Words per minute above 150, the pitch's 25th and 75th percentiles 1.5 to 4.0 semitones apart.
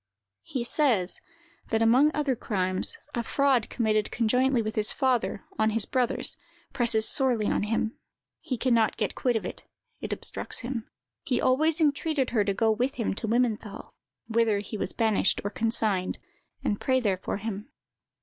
Yes: average, 170 wpm; average, 3.1 semitones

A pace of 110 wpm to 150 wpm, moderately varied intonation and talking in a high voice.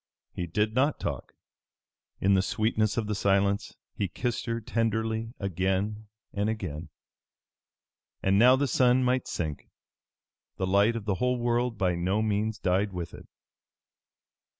No: average, 145 wpm; average, 3.2 semitones; low, 105 Hz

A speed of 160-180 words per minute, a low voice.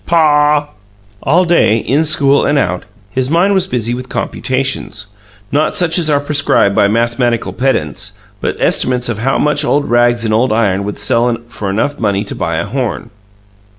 Yes: average, 175 wpm; low, 125 Hz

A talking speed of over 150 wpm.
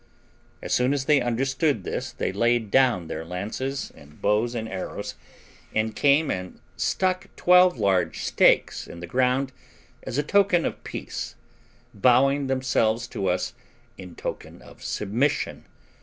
No: average, 140 wpm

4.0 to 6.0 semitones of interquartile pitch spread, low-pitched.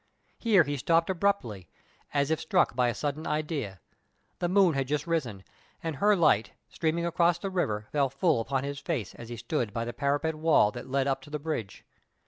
No: average, 5.2 semitones; medium, 145 Hz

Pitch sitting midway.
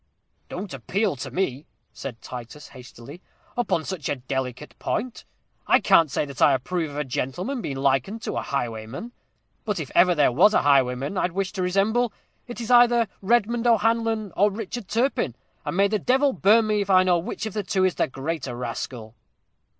Yes: medium, 180 Hz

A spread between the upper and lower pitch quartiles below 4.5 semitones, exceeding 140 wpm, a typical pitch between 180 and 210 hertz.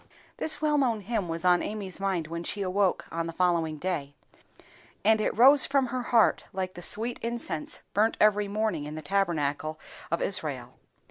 No: average, 4.9 semitones; average, 180 wpm; high, 190 Hz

